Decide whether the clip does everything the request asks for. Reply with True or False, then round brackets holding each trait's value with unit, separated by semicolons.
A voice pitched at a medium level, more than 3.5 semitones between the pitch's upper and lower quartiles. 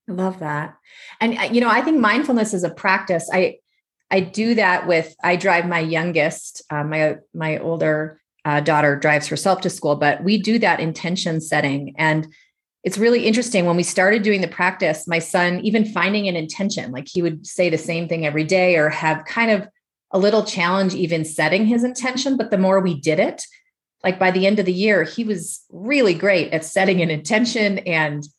True (180 Hz; 4.8 semitones)